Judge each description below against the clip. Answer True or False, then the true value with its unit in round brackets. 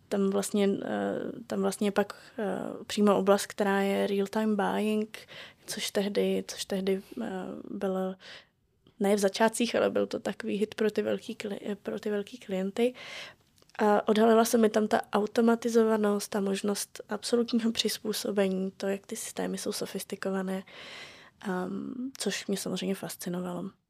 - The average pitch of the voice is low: False (205 Hz)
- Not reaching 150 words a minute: True (130 wpm)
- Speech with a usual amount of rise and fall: False (2.3 semitones)